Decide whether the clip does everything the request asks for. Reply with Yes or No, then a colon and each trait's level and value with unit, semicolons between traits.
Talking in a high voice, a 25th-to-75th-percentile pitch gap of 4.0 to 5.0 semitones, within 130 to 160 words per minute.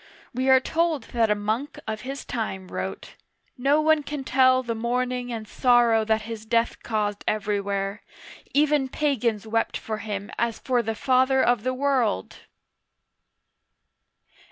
No: high, 235 Hz; average, 3.3 semitones; average, 150 wpm